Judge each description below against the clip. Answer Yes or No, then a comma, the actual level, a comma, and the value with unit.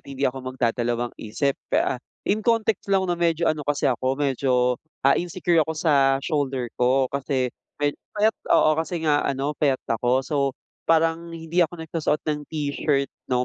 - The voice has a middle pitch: Yes, medium, 145 Hz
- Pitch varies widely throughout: No, average, 3.9 semitones